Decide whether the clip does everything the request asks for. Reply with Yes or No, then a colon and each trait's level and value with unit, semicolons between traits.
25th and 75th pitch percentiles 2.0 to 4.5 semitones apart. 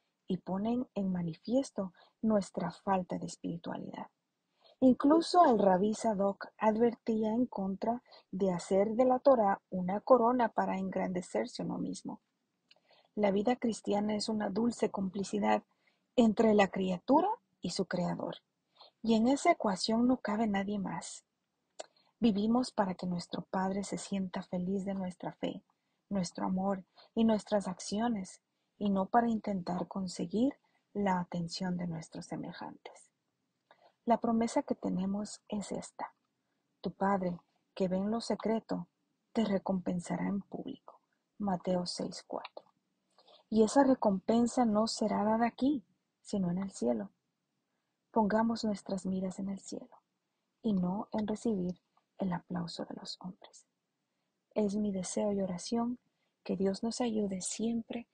Yes: average, 3.4 semitones